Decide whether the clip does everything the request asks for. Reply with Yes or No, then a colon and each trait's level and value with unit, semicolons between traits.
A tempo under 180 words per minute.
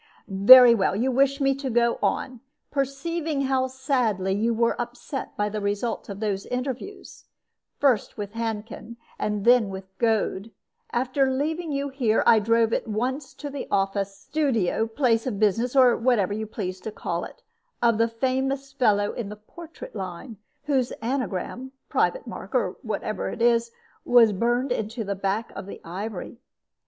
Yes: average, 165 wpm